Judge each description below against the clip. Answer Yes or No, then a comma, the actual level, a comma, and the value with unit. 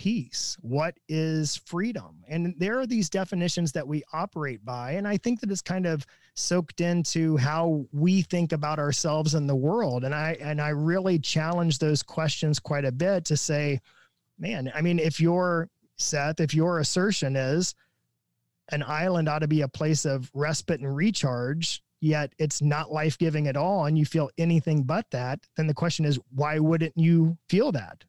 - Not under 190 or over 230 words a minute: No, average, 180 wpm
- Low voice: No, medium, 155 Hz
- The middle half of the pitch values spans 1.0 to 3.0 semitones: Yes, narrow, 2.6 semitones